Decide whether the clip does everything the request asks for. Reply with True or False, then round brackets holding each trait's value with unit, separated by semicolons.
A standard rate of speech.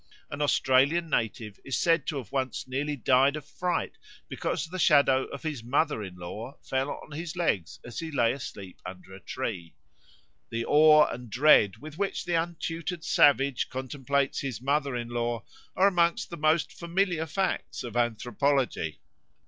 True (165 wpm)